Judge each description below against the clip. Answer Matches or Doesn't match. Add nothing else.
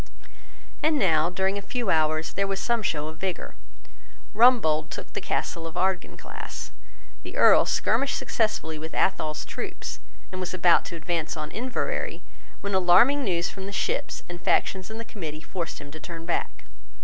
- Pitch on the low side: Doesn't match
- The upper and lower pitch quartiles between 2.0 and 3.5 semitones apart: Doesn't match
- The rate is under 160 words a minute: Doesn't match